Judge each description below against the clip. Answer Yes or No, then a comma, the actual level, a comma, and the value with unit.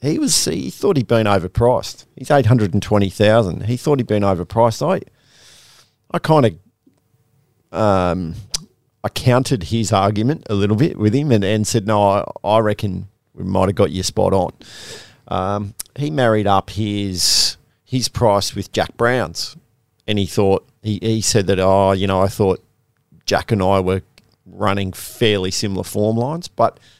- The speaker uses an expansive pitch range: No, average, 3.3 semitones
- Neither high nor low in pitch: No, low, 105 Hz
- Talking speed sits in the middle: Yes, average, 175 wpm